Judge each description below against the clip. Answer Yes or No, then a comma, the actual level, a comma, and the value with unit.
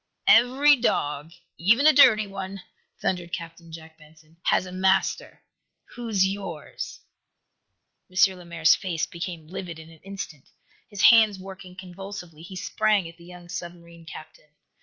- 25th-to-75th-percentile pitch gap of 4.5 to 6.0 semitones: No, average, 3.0 semitones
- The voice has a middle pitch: Yes, medium, 180 Hz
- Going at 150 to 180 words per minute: No, average, 140 wpm